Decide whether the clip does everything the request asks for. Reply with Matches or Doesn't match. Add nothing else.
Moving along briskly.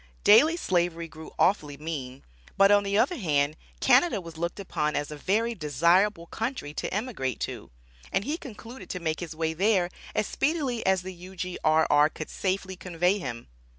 Doesn't match